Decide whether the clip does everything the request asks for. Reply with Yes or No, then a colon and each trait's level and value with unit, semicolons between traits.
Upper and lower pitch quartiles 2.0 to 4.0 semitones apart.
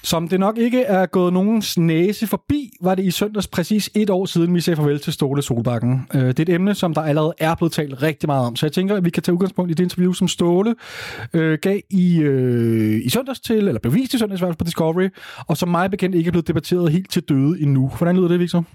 Yes: average, 3.2 semitones